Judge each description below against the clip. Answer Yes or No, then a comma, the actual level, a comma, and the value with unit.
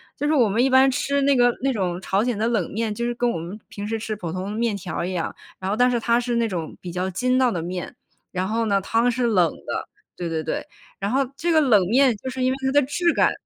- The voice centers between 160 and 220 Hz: No, high, 230 Hz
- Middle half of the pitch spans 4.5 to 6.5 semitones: Yes, average, 4.9 semitones